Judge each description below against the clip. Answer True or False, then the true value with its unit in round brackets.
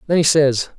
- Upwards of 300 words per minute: False (230 wpm)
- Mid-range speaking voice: True (150 Hz)